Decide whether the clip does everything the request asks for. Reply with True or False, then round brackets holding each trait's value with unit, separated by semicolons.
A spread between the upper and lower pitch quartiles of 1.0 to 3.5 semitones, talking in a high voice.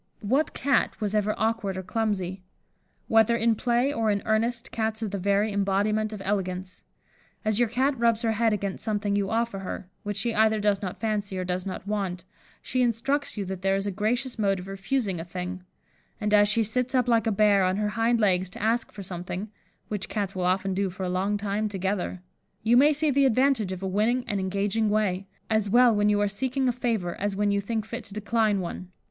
True (2.8 semitones; 210 Hz)